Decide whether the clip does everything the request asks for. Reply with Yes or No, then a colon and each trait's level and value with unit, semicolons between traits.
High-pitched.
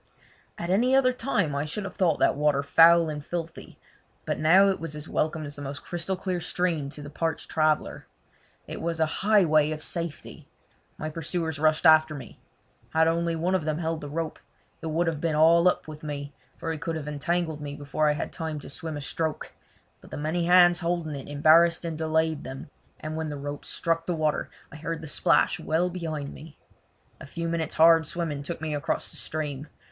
No: medium, 160 Hz